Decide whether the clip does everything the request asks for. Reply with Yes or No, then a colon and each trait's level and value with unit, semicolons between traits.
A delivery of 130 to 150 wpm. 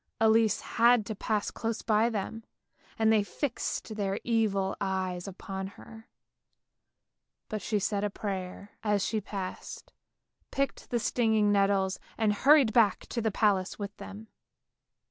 Yes: average, 140 wpm